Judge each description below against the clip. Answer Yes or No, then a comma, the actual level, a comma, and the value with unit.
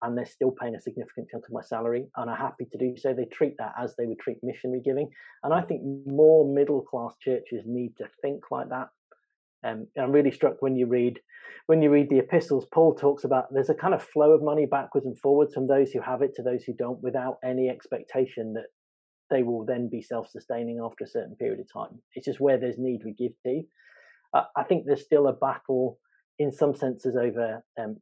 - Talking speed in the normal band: No, fast, 230 wpm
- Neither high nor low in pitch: No, low, 130 Hz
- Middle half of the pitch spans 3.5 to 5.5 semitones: No, narrow, 2.5 semitones